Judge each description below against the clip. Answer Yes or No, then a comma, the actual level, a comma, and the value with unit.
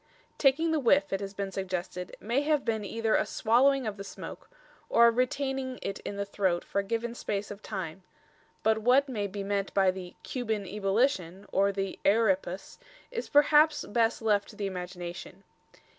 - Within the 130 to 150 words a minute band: No, average, 180 wpm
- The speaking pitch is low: No, high, 210 Hz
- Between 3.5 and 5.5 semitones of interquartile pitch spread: Yes, average, 4.3 semitones